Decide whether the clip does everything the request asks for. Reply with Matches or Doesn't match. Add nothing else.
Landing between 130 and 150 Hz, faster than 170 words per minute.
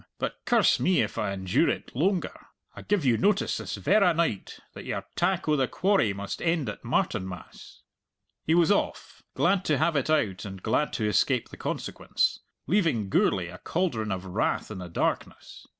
Matches